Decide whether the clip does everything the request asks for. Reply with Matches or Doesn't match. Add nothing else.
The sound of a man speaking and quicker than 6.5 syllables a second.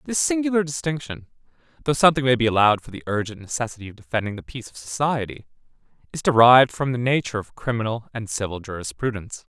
Matches